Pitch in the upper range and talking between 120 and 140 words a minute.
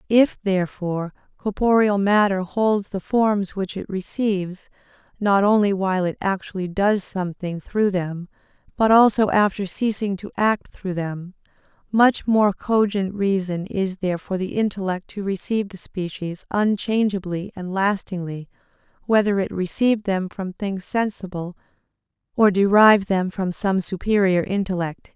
Yes: high, 195 Hz; slow, 135 wpm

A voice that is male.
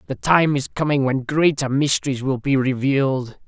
Yes: male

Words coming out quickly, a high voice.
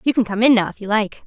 Yes: fast, 380 wpm; high, 220 Hz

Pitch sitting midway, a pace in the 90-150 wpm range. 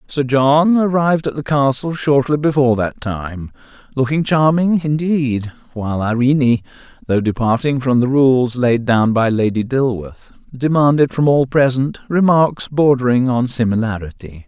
No: low, 130 Hz; slow, 135 wpm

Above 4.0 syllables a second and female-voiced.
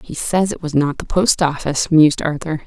Yes: 5.5 syllables/s; female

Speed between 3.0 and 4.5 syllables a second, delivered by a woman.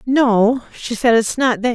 Yes: 4.0 syllables/s; female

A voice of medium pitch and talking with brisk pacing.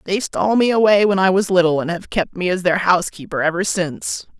Yes: medium, 175 Hz; fast, 230 wpm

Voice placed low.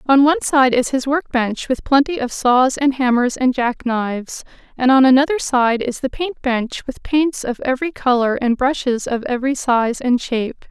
No: very high, 260 Hz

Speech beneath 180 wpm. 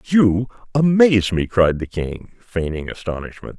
Yes: slow, 135 wpm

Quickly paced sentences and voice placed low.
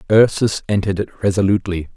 No: slow, 120 wpm; very low, 95 Hz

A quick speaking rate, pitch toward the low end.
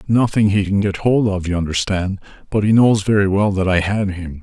Yes: fast, 230 wpm; low, 100 Hz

